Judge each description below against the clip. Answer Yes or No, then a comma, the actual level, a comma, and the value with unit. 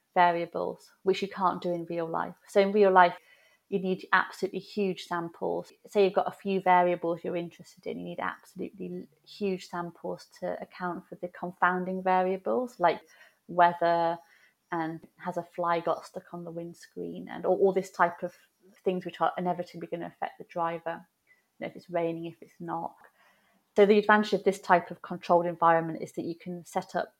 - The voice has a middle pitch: Yes, medium, 180 Hz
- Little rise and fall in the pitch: Yes, narrow, 1.8 semitones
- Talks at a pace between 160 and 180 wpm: No, average, 190 wpm